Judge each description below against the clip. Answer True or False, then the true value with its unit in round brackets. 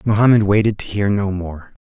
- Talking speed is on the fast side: False (195 wpm)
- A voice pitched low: True (100 Hz)